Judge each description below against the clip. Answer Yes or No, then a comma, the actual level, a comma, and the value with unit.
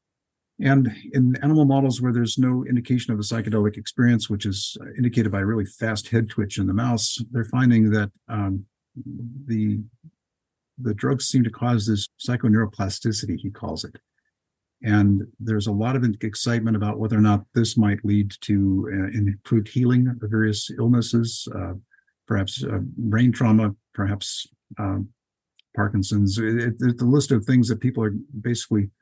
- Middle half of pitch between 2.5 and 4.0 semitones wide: Yes, average, 2.8 semitones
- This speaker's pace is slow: No, average, 160 wpm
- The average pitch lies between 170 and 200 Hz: No, low, 110 Hz